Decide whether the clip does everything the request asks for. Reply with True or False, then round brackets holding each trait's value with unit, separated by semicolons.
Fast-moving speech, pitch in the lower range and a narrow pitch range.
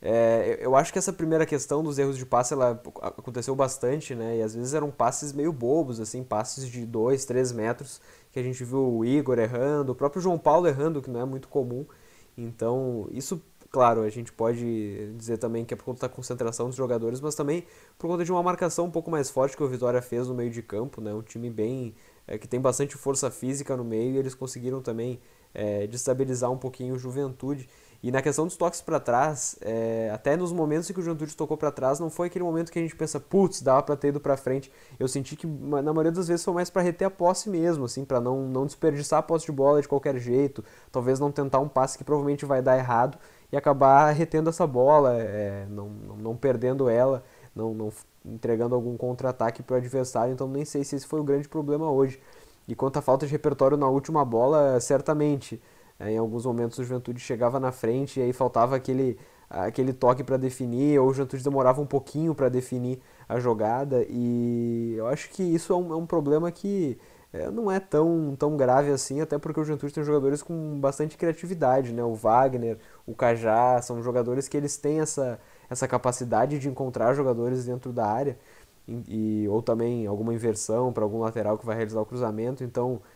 False (215 wpm; 130 Hz; 3.5 semitones)